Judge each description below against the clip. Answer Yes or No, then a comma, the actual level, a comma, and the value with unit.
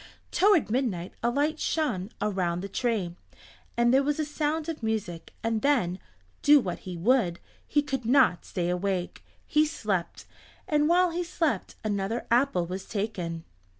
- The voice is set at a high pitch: Yes, high, 230 Hz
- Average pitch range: No, wide, 8.0 semitones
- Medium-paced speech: Yes, average, 155 wpm